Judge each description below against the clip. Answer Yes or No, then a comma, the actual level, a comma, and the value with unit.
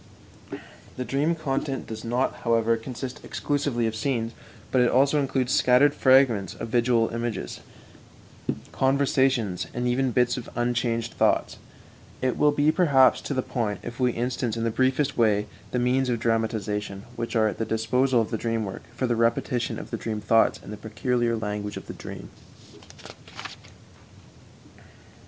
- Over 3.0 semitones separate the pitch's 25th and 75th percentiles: No, narrow, 2.6 semitones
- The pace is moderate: Yes, average, 160 wpm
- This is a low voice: Yes, low, 120 Hz